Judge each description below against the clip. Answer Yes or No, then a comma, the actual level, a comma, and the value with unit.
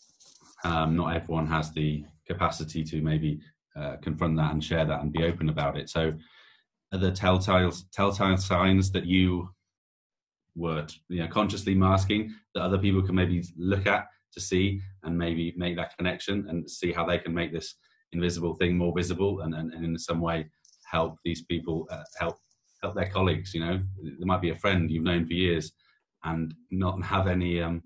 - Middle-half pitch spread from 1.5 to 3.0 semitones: Yes, narrow, 2.4 semitones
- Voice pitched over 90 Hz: No, very low, 85 Hz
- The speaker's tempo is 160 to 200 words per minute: Yes, average, 185 wpm